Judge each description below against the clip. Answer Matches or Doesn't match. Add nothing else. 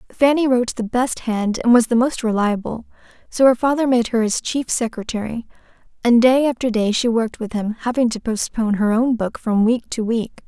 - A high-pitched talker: Matches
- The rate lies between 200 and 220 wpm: Matches